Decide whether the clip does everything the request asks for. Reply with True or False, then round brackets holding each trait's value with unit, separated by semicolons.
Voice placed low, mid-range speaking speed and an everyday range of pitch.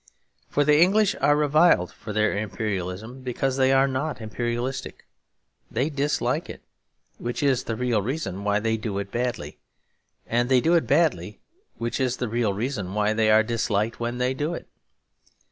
True (120 Hz; 170 wpm; 4.1 semitones)